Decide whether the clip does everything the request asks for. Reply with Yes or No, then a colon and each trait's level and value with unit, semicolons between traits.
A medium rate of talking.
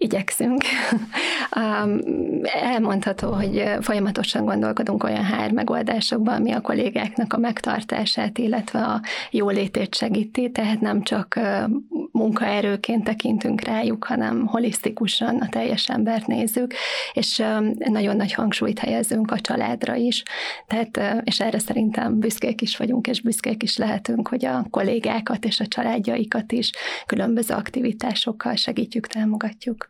Yes: average, 120 wpm